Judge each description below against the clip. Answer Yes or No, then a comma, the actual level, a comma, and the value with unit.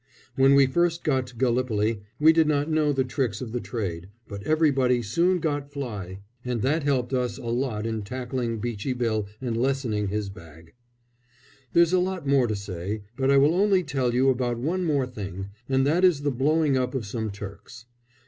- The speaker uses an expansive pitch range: No, average, 4.7 semitones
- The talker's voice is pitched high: No, low, 125 Hz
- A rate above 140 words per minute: Yes, average, 195 wpm